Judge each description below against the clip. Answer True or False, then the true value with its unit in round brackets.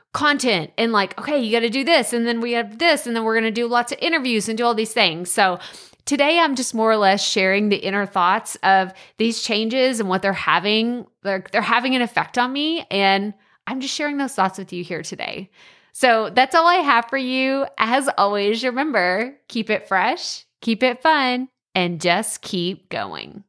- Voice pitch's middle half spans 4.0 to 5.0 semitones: True (4.5 semitones)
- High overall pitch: True (230 Hz)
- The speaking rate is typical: False (215 wpm)